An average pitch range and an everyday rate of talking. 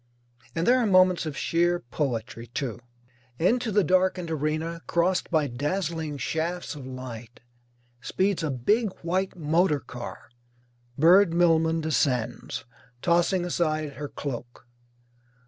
No: average, 4.2 semitones; slow, 120 wpm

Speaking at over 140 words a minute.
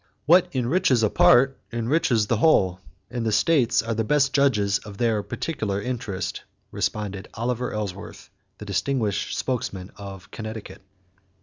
No: slow, 135 wpm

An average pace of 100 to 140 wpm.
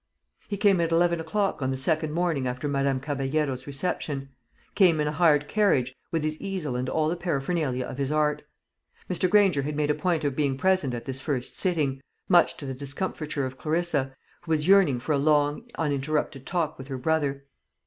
No: average, 195 wpm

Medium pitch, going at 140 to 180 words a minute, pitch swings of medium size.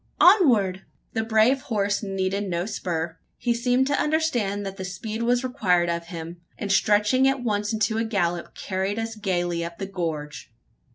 No: high, 205 Hz; average, 165 wpm; average, 4.5 semitones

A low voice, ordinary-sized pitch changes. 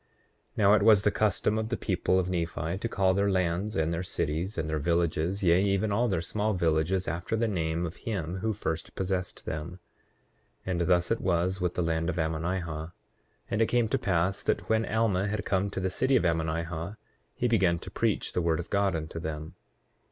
Yes: very low, 90 Hz; average, 3.4 semitones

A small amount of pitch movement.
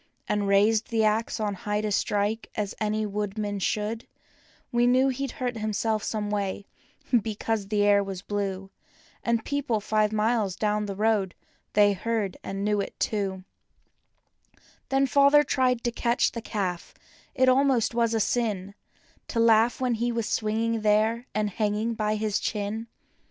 Yes: narrow, 2.1 semitones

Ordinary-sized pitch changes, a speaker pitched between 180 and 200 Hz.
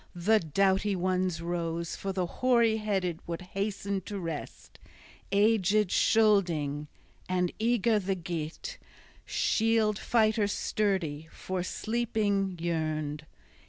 Yes: average, 3.9 semitones; high, 190 Hz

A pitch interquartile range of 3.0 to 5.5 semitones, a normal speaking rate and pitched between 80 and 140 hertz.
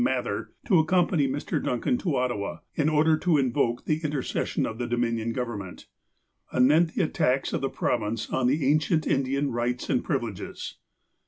Yes: average, 4.4 semitones; average, 160 wpm; low, 135 Hz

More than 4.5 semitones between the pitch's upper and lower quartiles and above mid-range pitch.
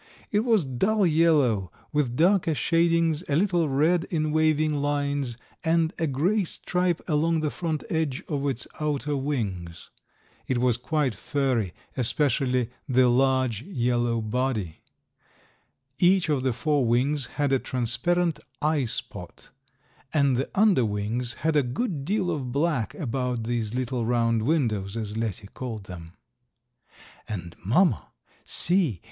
No: average, 5.1 semitones; low, 135 Hz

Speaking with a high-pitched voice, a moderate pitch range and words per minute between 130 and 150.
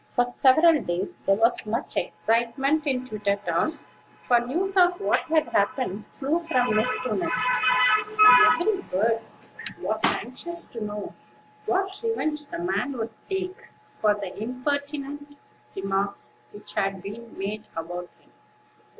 No: very high, 250 Hz; wide, 7.0 semitones; slow, 135 wpm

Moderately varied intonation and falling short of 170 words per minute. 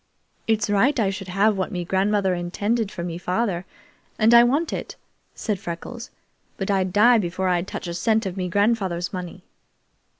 No: average, 3.4 semitones; average, 175 wpm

